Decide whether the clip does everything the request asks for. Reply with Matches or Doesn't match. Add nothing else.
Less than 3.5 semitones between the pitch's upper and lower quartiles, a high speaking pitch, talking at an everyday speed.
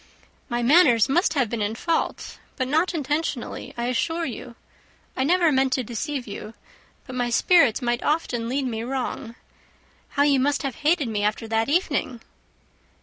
Doesn't match